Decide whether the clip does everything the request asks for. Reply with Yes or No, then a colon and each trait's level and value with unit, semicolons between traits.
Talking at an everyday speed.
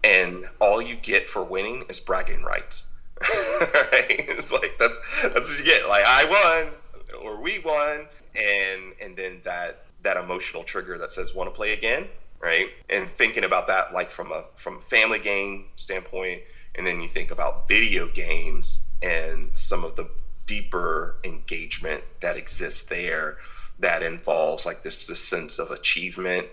Yes: average, 165 wpm